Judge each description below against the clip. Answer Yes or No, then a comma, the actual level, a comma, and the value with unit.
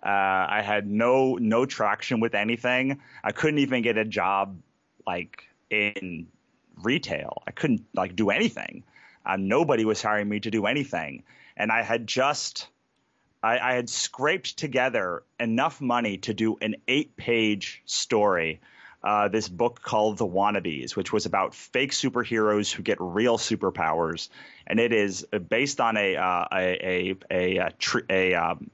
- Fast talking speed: No, average, 155 wpm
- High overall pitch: No, low, 105 Hz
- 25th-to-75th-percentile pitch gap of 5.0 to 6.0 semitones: No, average, 3.5 semitones